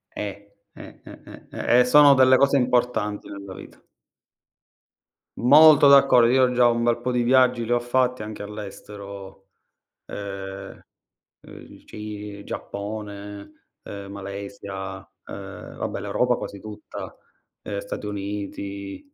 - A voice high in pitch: No, low, 105 Hz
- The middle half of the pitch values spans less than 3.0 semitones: No, average, 3.7 semitones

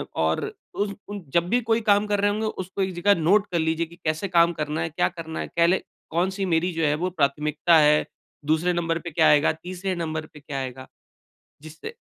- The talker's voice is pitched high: No, medium, 170 Hz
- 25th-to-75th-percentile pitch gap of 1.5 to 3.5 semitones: Yes, average, 3.2 semitones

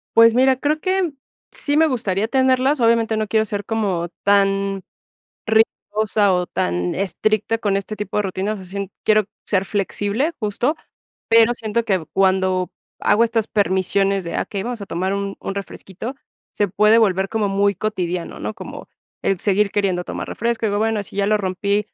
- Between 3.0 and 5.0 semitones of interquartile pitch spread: No, narrow, 2.4 semitones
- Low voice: No, high, 205 Hz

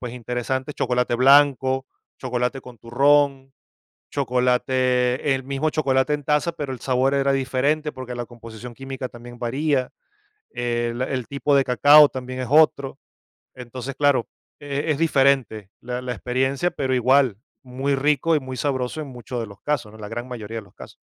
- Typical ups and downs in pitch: No, narrow, 2.1 semitones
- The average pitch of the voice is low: Yes, low, 130 Hz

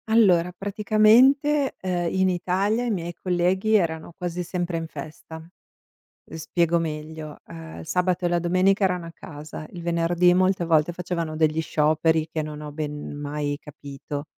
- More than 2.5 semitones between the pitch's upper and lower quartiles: Yes, average, 2.9 semitones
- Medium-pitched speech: Yes, medium, 170 Hz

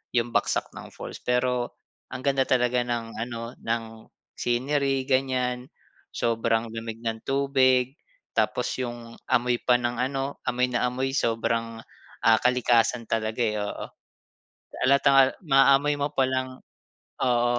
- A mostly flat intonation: Yes, narrow, 2.2 semitones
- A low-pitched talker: Yes, low, 125 Hz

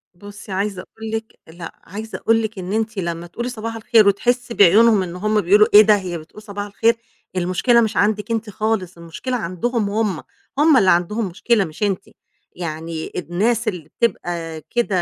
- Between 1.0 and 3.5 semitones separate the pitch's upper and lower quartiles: No, average, 3.9 semitones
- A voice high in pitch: Yes, high, 205 Hz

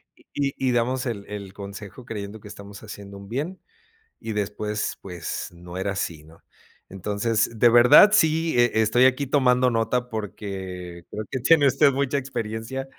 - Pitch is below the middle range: Yes, low, 110 Hz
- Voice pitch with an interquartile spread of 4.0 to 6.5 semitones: Yes, average, 4.3 semitones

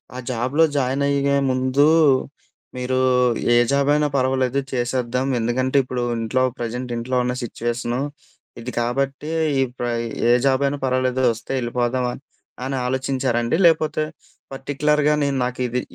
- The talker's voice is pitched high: No, low, 130 Hz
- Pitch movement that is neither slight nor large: No, narrow, 2.0 semitones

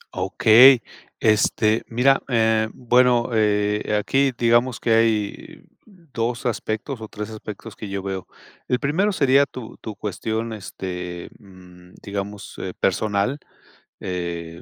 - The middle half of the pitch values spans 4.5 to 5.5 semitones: No, average, 3.6 semitones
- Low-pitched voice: Yes, low, 110 Hz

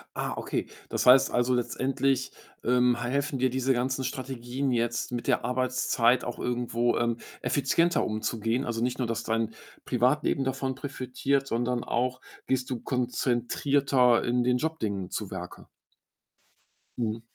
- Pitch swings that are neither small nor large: No, narrow, 1.8 semitones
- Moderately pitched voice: No, low, 125 Hz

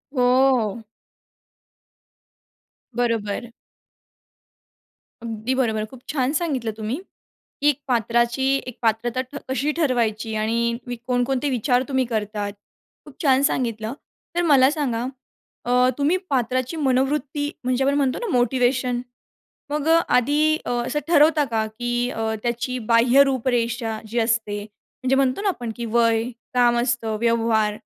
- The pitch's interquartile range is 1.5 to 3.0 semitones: Yes, average, 2.7 semitones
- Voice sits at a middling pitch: No, high, 245 Hz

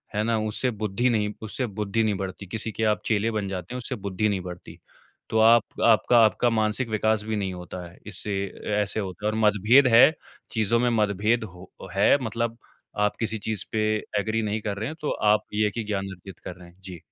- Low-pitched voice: Yes, low, 105 Hz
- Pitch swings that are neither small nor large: No, narrow, 2.2 semitones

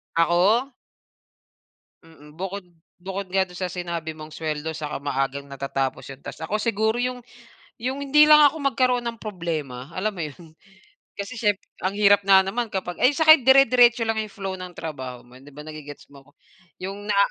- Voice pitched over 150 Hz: Yes, high, 190 Hz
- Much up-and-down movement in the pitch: Yes, wide, 6.6 semitones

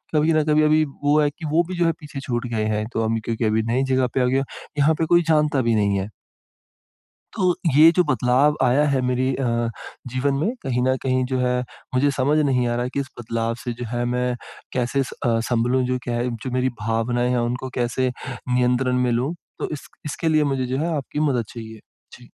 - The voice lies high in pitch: No, low, 130 Hz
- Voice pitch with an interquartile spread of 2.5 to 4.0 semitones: Yes, average, 3.2 semitones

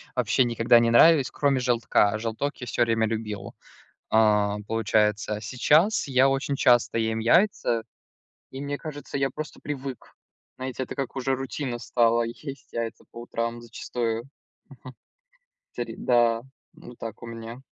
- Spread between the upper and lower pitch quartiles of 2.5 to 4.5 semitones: Yes, average, 2.9 semitones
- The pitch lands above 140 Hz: No, low, 120 Hz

